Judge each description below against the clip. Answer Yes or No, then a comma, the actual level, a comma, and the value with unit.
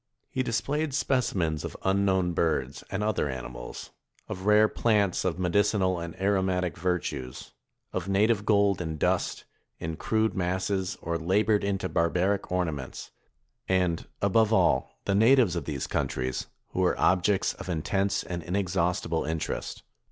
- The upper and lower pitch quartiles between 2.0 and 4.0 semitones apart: Yes, average, 3.3 semitones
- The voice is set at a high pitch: No, very low, 95 Hz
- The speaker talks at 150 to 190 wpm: No, slow, 135 wpm